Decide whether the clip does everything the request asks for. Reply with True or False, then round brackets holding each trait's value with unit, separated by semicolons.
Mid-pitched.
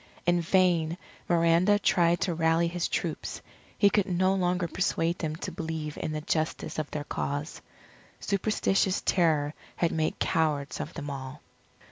True (165 Hz)